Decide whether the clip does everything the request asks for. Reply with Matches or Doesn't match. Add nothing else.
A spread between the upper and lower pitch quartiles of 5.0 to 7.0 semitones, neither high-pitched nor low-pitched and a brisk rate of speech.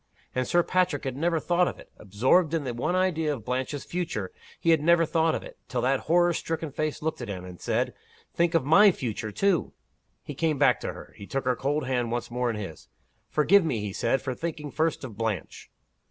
Matches